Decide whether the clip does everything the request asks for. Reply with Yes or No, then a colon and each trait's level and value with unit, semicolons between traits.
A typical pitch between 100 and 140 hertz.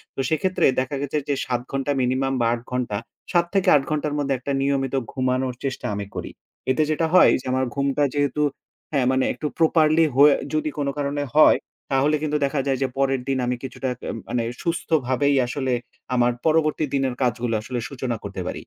Yes: low, 135 Hz